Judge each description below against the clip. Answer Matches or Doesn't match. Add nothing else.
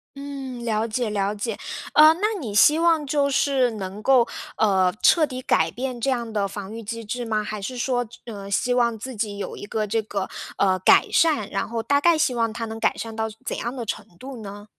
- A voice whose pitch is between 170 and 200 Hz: Doesn't match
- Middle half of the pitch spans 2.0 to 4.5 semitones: Matches